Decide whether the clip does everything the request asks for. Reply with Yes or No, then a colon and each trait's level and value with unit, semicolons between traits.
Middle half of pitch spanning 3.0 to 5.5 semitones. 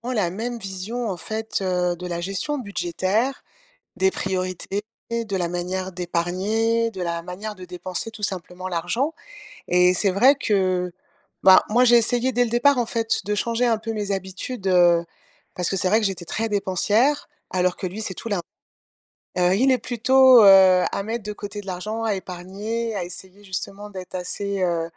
Yes: average, 3.7 semitones